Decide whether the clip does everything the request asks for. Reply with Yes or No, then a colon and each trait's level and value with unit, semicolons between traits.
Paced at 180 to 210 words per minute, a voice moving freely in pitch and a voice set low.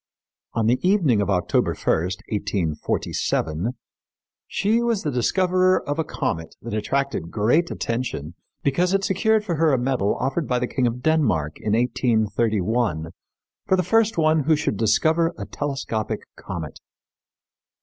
No: average, 145 wpm; wide, 7.5 semitones; low, 125 Hz